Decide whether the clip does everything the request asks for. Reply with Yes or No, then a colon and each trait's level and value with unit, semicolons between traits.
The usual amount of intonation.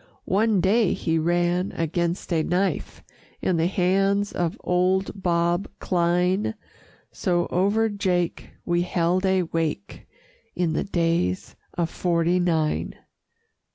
No: narrow, 2.0 semitones